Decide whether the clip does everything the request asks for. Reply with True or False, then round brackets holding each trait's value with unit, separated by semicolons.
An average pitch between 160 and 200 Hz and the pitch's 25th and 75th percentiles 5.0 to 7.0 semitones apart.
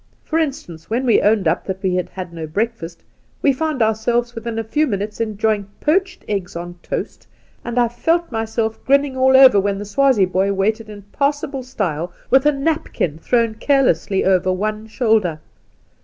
False (220 Hz; 5.3 semitones)